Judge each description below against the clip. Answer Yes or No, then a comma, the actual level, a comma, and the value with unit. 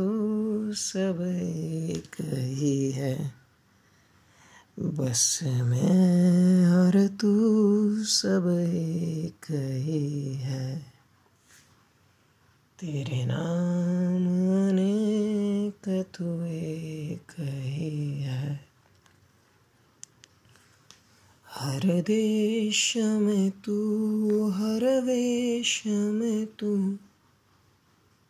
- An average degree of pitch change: No, wide, 7.5 semitones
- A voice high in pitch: No, medium, 165 Hz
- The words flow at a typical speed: No, slow, 55 wpm